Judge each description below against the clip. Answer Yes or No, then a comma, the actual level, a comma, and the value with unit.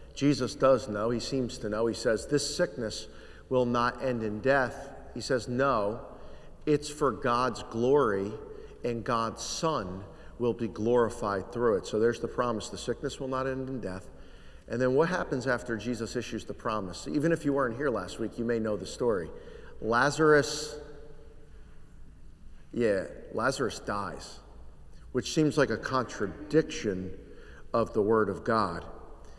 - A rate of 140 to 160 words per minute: Yes, average, 155 wpm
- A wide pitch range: No, average, 4.8 semitones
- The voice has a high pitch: No, low, 120 Hz